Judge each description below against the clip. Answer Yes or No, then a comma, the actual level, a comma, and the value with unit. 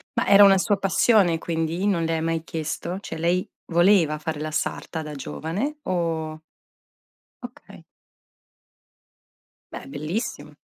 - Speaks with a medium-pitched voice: Yes, medium, 165 Hz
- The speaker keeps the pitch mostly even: No, average, 3.2 semitones